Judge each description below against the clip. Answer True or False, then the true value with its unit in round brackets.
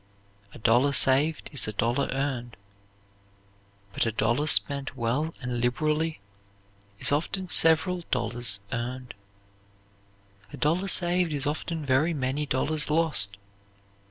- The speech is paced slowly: True (120 wpm)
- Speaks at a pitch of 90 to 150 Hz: True (140 Hz)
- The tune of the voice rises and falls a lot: False (4.5 semitones)